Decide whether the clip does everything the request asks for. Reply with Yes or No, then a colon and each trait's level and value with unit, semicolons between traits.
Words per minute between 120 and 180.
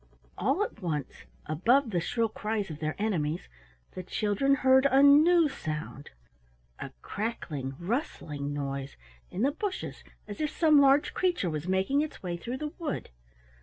Yes: average, 155 wpm